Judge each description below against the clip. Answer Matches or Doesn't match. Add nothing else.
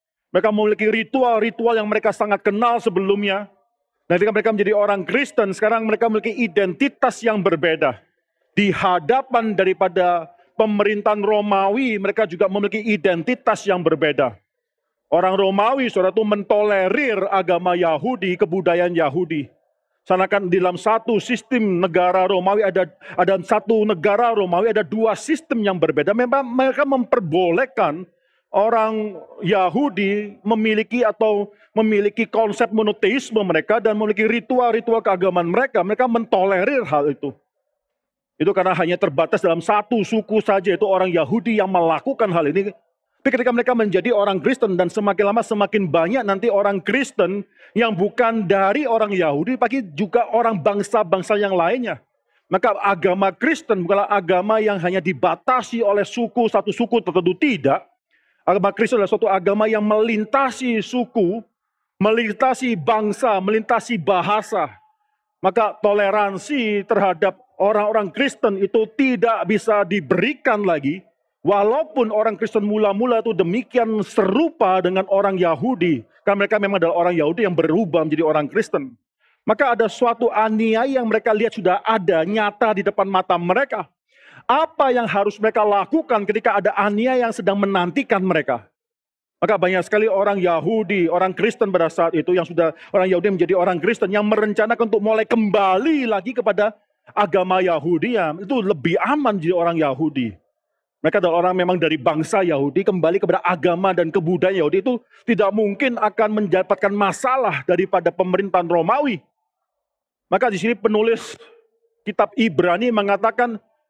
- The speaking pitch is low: Doesn't match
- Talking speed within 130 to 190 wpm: Matches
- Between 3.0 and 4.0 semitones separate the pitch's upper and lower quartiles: Matches